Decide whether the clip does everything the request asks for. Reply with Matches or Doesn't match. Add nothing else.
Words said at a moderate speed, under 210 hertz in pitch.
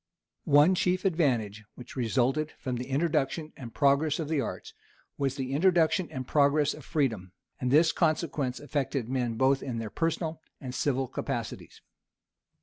Matches